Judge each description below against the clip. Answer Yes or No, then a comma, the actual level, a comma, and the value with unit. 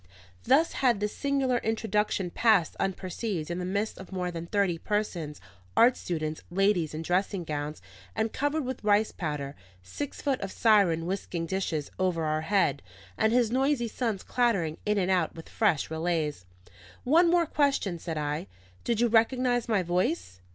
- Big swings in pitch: Yes, wide, 5.8 semitones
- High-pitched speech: Yes, high, 195 Hz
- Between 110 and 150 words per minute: No, average, 165 wpm